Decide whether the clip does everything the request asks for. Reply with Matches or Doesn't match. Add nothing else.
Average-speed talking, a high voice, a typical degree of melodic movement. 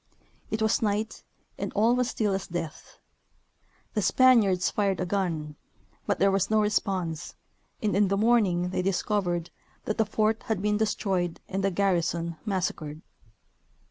Matches